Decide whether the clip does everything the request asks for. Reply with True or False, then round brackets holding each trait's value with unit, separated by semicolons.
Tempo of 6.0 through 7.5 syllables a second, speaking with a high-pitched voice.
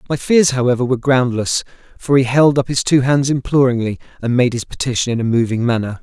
False (6.1 syllables/s; 125 Hz)